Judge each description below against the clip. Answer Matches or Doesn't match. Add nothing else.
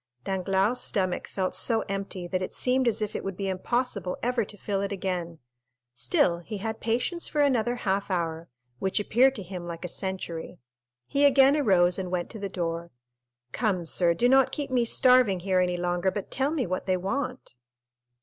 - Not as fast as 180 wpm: Doesn't match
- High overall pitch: Matches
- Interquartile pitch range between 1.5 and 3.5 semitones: Doesn't match